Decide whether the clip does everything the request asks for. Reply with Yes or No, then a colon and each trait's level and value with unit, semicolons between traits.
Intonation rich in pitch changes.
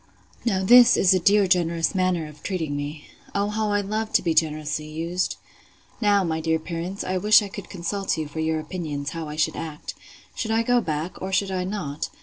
No: average, 4.1 semitones